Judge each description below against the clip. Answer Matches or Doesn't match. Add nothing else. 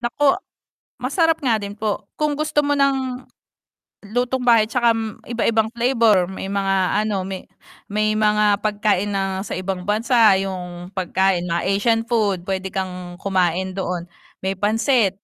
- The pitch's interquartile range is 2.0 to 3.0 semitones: Doesn't match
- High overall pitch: Matches